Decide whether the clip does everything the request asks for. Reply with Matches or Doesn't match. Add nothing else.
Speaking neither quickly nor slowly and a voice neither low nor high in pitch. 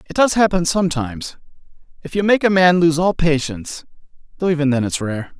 Matches